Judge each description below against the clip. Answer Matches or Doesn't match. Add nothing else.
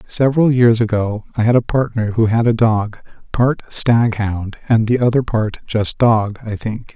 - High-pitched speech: Doesn't match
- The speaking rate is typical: Matches